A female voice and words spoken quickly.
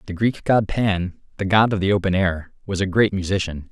No: male; fast, 225 wpm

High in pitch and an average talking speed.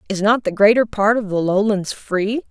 No: high, 205 Hz; fast, 215 wpm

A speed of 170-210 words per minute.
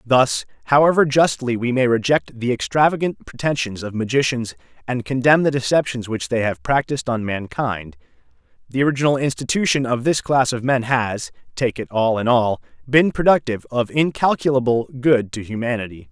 No: average, 155 wpm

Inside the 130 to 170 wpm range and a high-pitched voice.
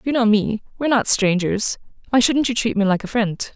No: average, 200 wpm; high, 225 Hz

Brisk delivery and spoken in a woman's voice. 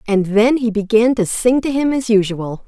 Yes: fast, 225 wpm; female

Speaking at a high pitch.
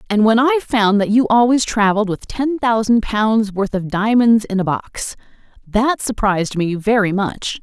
Yes: high, 215 Hz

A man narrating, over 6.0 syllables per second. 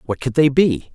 No: male; 4.9 syllables/s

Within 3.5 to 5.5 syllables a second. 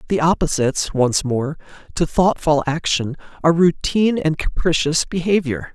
Yes: 4.9 syllables/s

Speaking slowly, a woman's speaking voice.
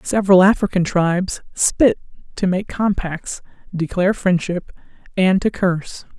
Yes: slow, 115 wpm; female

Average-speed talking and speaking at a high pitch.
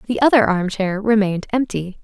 Yes: average, 175 wpm; high, 210 Hz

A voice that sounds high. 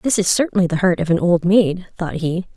No: medium, 180 Hz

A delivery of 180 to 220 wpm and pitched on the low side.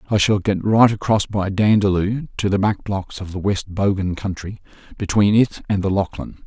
Yes: average, 195 wpm; low, 100 Hz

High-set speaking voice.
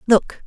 Yes: high, 225 Hz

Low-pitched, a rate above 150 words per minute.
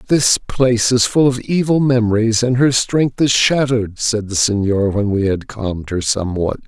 Yes: low, 115 Hz; average, 190 wpm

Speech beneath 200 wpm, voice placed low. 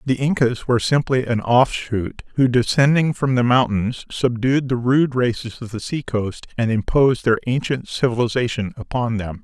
Yes: average, 165 wpm; low, 120 Hz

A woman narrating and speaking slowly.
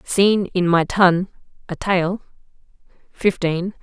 Yes: female; slow, 110 wpm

